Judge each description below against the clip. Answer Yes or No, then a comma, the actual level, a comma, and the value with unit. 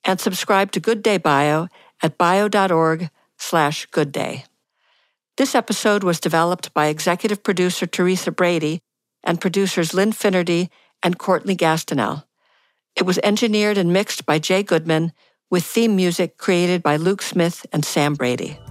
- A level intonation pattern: No, average, 3.4 semitones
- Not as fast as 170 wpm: Yes, average, 140 wpm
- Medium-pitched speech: Yes, medium, 180 Hz